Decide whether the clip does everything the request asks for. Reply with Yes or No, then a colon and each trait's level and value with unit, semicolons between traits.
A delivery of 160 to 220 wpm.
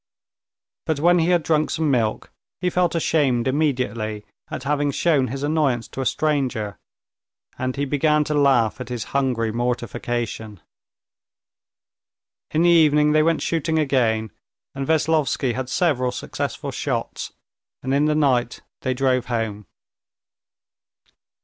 No: slow, 135 wpm